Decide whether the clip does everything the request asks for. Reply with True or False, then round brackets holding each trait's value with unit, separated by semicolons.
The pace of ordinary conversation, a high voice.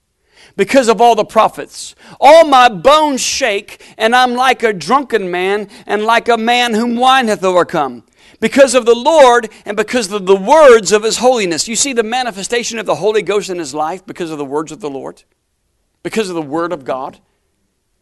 True (195 wpm; 220 Hz)